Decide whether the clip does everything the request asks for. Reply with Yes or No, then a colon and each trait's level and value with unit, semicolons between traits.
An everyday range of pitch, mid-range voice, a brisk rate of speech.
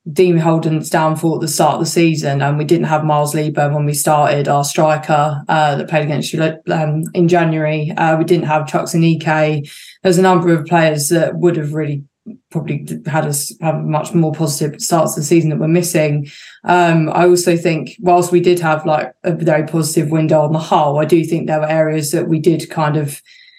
No: narrow, 1.8 semitones; medium, 160 Hz; fast, 220 wpm